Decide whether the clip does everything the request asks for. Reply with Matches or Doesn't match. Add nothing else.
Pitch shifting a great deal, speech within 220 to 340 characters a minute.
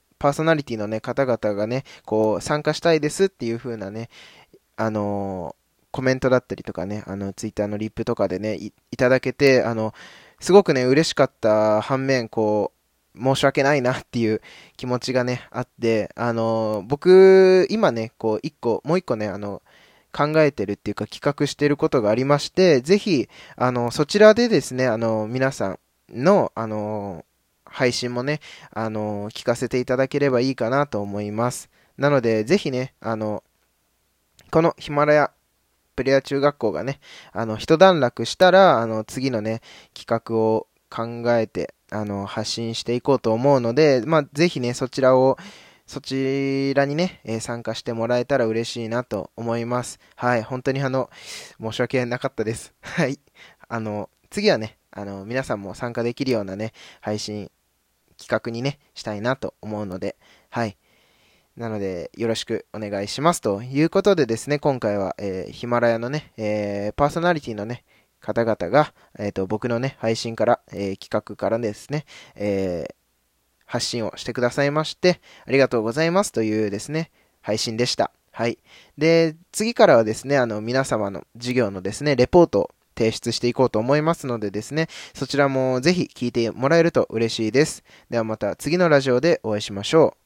Doesn't match